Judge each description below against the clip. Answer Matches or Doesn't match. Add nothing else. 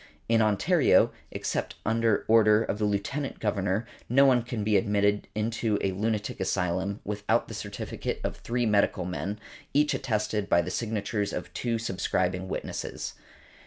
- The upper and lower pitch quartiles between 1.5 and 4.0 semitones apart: Matches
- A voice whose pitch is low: Matches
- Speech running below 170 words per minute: Matches